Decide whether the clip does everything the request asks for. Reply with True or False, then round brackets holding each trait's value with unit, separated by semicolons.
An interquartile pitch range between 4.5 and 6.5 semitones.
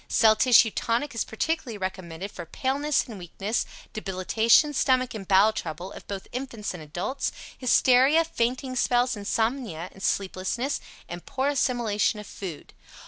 True (5.1 semitones)